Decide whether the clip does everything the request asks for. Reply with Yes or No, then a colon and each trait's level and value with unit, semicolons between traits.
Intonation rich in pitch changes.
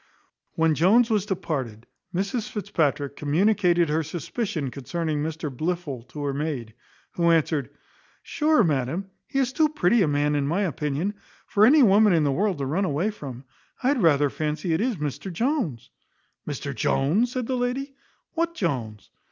Yes: wide, 6.6 semitones